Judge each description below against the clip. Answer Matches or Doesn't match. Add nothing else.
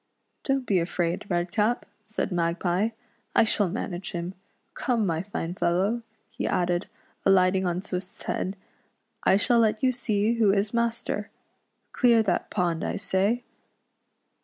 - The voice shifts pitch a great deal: Doesn't match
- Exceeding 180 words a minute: Doesn't match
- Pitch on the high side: Matches